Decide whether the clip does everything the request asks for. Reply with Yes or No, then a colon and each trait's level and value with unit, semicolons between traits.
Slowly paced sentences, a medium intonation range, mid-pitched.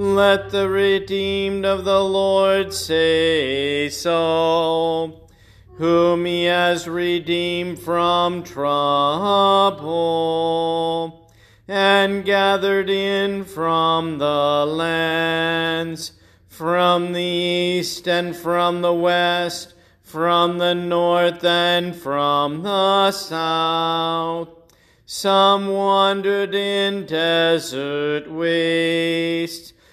Yes: slow, 80 wpm; average, 3.0 semitones; medium, 170 Hz